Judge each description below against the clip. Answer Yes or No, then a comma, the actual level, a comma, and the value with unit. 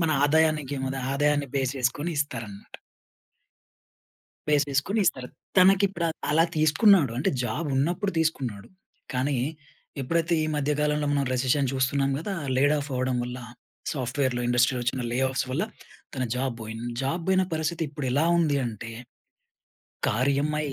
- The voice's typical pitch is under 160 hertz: Yes, medium, 140 Hz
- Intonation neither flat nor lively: Yes, average, 3.4 semitones